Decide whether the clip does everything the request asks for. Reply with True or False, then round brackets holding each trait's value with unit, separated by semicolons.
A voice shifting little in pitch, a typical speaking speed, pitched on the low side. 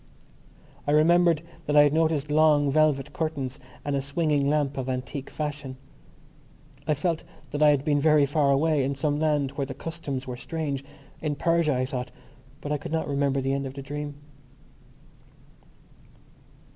False (1.9 semitones; 165 wpm; 145 Hz)